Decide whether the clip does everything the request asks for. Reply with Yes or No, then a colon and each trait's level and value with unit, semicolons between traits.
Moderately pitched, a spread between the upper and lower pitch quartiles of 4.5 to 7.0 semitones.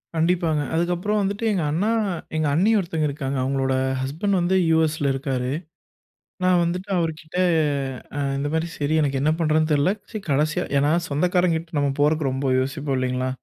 No: medium, 155 Hz; average, 3.7 semitones